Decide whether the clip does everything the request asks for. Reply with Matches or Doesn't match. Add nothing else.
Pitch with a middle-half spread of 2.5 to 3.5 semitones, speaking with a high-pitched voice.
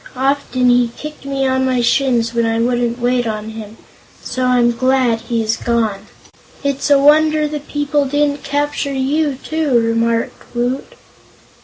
Matches